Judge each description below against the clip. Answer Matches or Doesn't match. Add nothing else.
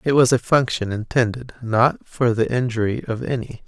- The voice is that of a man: Matches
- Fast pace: Doesn't match